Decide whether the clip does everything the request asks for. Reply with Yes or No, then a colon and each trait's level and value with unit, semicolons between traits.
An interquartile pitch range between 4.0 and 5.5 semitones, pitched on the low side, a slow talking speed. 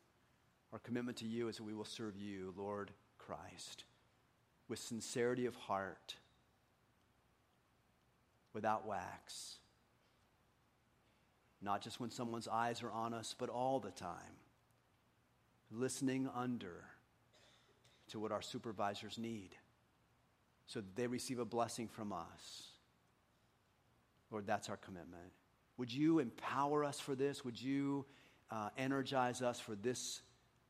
No: average, 3.3 semitones; low, 115 Hz; slow, 125 wpm